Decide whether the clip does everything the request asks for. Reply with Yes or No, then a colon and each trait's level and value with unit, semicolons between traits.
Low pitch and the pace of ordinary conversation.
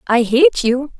No: very high, 270 Hz; average, 180 wpm